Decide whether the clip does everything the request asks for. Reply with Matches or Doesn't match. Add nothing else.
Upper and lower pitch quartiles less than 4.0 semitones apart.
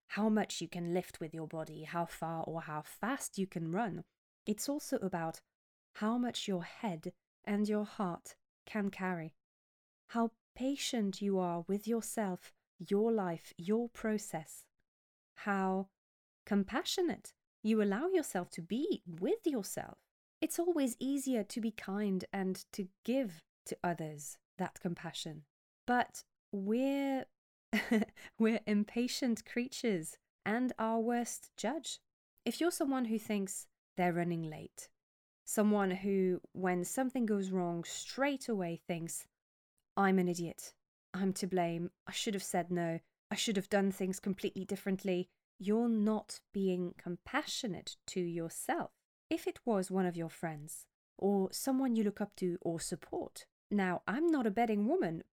Doesn't match